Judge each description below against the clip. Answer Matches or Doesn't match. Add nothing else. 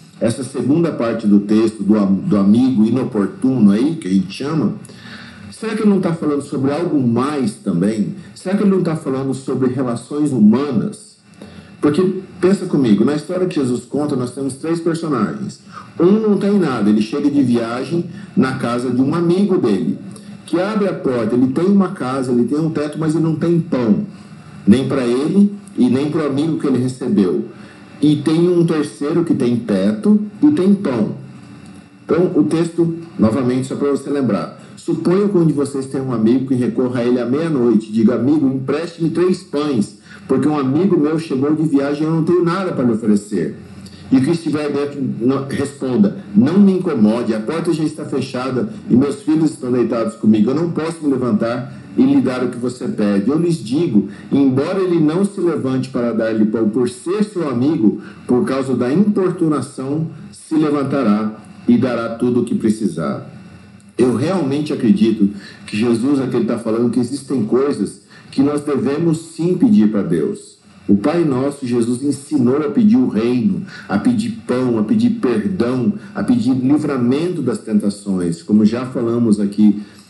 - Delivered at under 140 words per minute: Doesn't match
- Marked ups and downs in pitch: Matches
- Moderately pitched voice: Matches